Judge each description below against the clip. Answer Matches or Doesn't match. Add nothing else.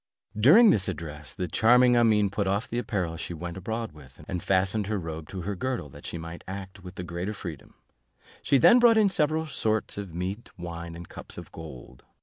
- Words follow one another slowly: Doesn't match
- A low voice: Matches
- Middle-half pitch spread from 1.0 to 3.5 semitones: Doesn't match